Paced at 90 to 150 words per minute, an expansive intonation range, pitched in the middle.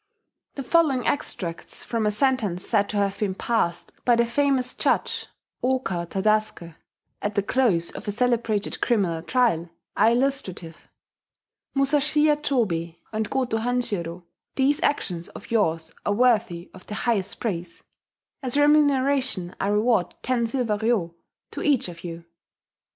No: average, 140 wpm; wide, 5.9 semitones; high, 220 Hz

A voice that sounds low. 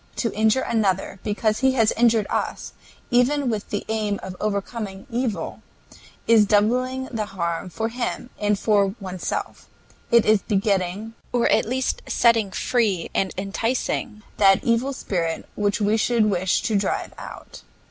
No: high, 215 Hz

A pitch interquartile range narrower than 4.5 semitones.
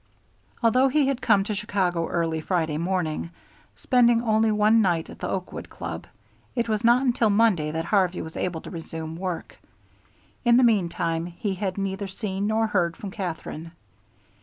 No: average, 4.8 semitones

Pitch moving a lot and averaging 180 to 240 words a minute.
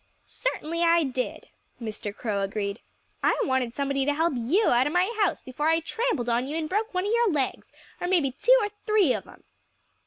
Yes: wide, 6.6 semitones; fast, 205 wpm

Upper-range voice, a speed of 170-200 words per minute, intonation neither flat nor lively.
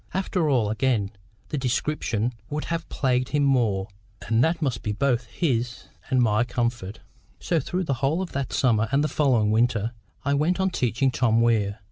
No: low, 125 Hz; average, 180 wpm; average, 4.3 semitones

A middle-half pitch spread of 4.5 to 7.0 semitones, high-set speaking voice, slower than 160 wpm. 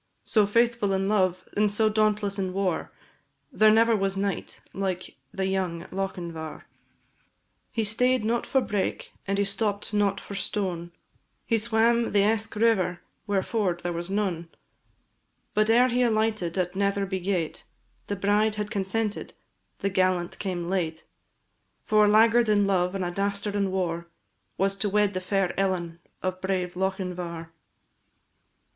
No: narrow, 2.5 semitones; high, 195 Hz; average, 150 wpm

